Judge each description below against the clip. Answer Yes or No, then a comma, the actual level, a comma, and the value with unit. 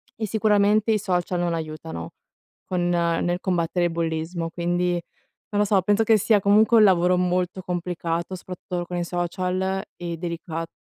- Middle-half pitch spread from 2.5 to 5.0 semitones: No, narrow, 2.1 semitones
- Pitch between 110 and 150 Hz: No, medium, 180 Hz